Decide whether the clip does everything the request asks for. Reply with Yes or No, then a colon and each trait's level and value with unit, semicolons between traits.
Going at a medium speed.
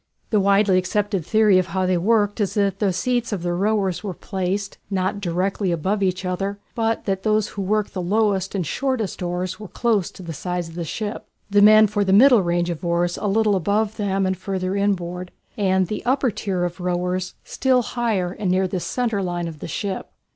No: fast, 210 wpm